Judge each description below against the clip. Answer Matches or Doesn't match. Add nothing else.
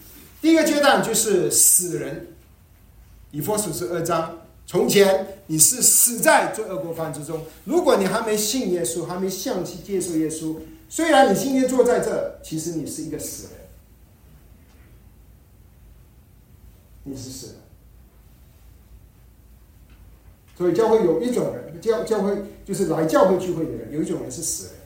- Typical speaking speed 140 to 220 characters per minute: Matches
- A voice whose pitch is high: Doesn't match